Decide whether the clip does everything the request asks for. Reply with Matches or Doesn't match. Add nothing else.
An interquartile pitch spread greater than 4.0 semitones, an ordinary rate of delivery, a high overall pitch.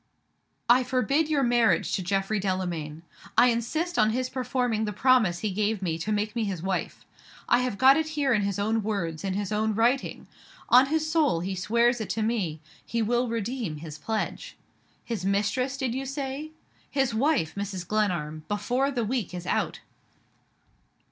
Matches